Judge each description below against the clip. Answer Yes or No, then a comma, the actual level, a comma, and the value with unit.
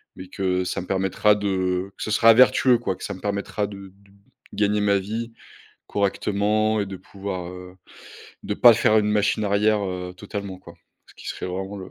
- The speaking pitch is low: Yes, low, 100 Hz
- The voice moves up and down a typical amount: No, narrow, 1.9 semitones